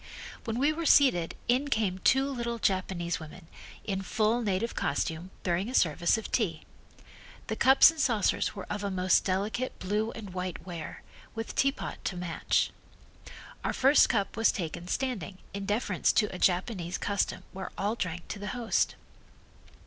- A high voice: Yes, high, 200 Hz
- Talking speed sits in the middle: Yes, average, 165 wpm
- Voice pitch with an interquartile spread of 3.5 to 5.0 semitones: Yes, average, 4.6 semitones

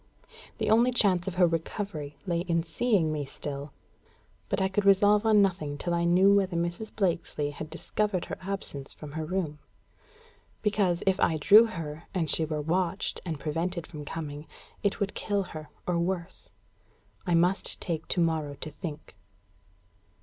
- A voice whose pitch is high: No, medium, 170 Hz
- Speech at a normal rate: Yes, average, 165 wpm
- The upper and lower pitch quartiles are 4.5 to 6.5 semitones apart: No, average, 3.8 semitones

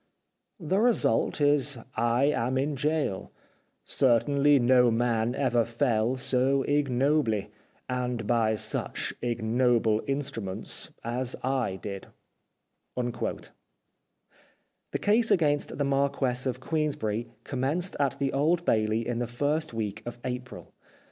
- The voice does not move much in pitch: No, average, 3.5 semitones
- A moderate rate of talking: No, slow, 115 wpm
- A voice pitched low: Yes, low, 125 Hz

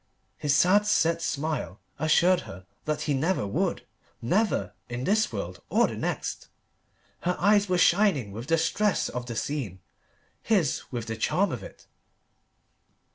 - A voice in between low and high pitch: Yes, medium, 155 Hz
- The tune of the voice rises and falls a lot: Yes, wide, 7.6 semitones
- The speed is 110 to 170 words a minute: Yes, average, 150 wpm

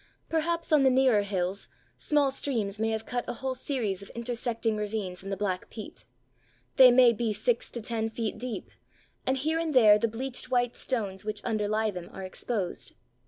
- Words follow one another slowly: No, average, 185 wpm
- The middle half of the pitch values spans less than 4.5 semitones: Yes, average, 3.6 semitones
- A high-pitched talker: Yes, high, 225 Hz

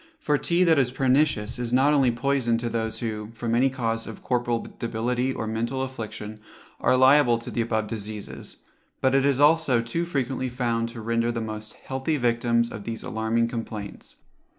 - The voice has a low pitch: Yes, low, 120 Hz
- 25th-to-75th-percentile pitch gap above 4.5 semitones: No, average, 2.7 semitones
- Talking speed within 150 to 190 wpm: Yes, average, 180 wpm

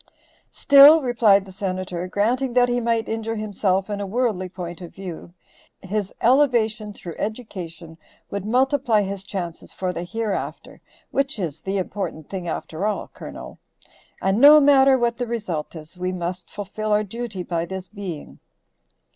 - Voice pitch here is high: Yes, high, 200 Hz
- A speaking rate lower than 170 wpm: Yes, average, 155 wpm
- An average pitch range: Yes, average, 4.3 semitones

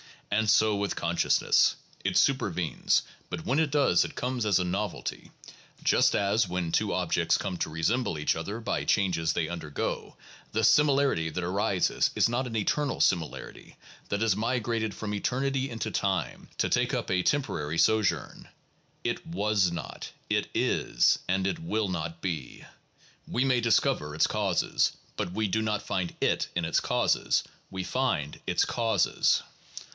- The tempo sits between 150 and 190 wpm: Yes, average, 160 wpm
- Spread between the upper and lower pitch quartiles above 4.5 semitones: Yes, average, 4.9 semitones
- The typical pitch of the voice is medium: No, low, 100 Hz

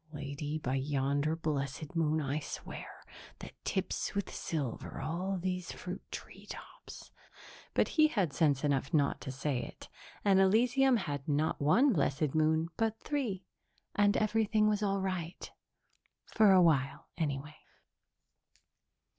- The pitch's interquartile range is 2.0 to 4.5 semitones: No, wide, 5.6 semitones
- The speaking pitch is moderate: Yes, medium, 160 Hz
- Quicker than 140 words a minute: No, slow, 135 wpm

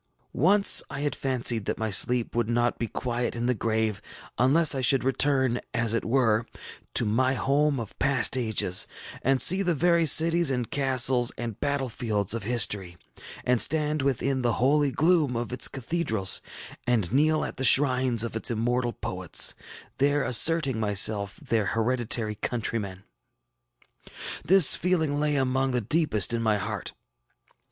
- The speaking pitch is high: No, low, 125 Hz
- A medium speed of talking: Yes, average, 155 wpm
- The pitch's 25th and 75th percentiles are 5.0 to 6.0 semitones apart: No, average, 3.8 semitones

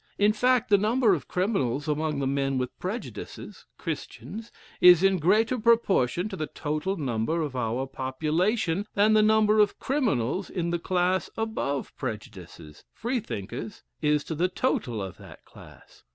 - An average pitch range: No, wide, 7.7 semitones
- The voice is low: No, medium, 175 Hz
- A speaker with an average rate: Yes, average, 150 wpm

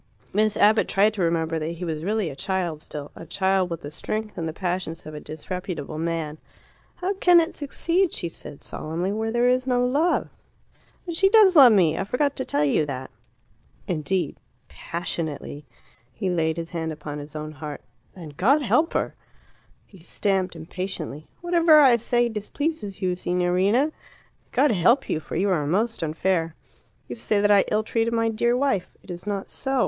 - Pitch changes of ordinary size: No, wide, 6.5 semitones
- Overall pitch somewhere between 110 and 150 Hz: No, high, 190 Hz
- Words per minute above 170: Yes, average, 185 wpm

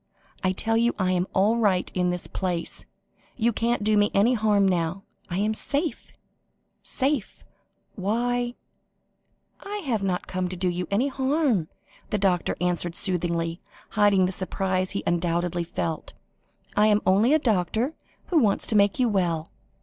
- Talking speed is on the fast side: No, average, 160 wpm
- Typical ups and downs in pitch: Yes, average, 4.2 semitones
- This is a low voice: No, high, 200 Hz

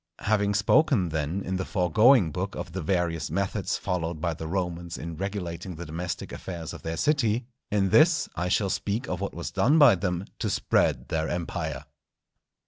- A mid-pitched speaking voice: No, very low, 90 Hz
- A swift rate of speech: No, average, 180 wpm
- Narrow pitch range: No, average, 3.3 semitones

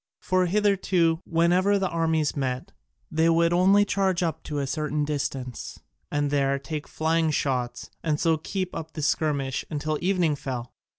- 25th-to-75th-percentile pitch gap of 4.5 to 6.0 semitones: No, average, 3.4 semitones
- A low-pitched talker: No, medium, 160 Hz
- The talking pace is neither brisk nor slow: Yes, average, 160 wpm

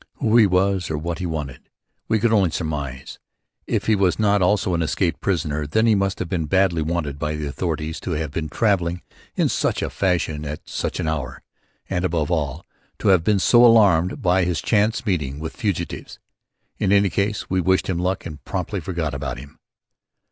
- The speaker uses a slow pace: No, average, 200 wpm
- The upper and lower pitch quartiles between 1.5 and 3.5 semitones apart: No, average, 4.1 semitones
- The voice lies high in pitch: No, very low, 90 Hz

